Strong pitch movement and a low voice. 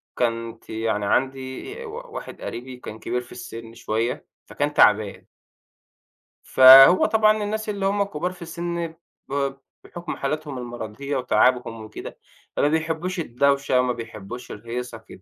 Yes: wide, 6.4 semitones; low, 130 Hz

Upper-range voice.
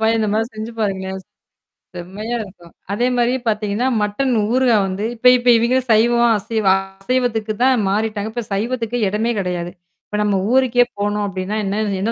Yes: high, 220 Hz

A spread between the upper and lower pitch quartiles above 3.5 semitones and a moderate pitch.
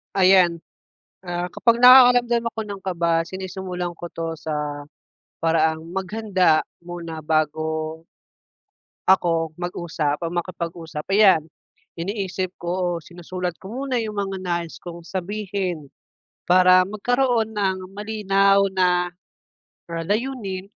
No: average, 3.0 semitones; medium, 180 Hz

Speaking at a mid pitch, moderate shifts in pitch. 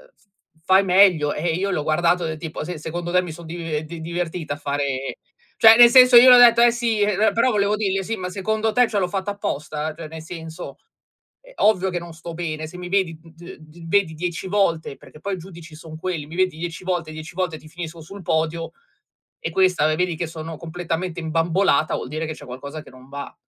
Yes: medium, 170 Hz; average, 3.3 semitones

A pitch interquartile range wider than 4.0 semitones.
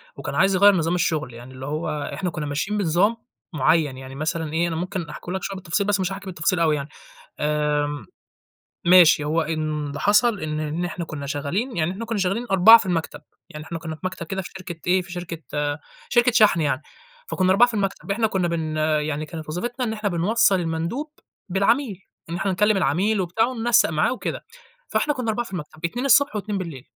Yes: average, 4.7 semitones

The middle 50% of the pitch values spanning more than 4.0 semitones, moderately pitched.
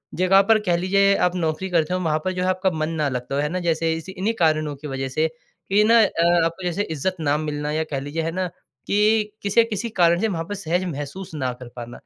No: average, 3.7 semitones; medium, 170 Hz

